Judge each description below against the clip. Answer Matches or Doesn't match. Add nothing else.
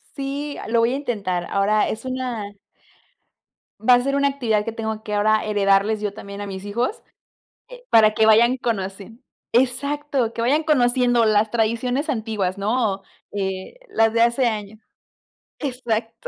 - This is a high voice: Matches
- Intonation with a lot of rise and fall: Doesn't match